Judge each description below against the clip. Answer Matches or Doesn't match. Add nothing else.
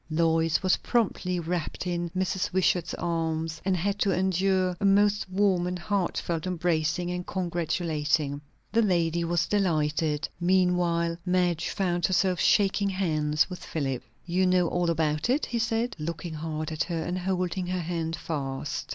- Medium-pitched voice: Matches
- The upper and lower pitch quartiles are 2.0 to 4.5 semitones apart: Matches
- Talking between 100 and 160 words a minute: Matches